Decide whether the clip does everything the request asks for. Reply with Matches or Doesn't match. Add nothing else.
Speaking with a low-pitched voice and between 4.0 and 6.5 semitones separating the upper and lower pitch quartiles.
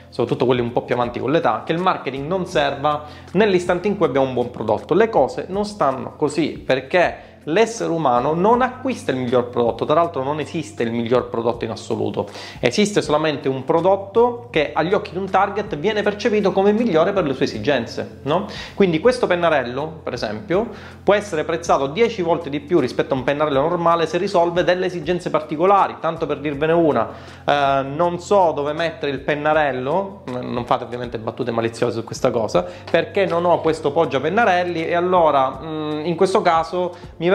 Doesn't match